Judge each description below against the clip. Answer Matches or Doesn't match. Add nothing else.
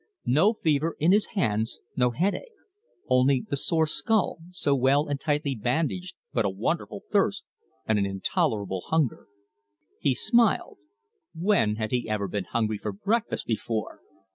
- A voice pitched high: Doesn't match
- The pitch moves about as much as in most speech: Doesn't match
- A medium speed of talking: Matches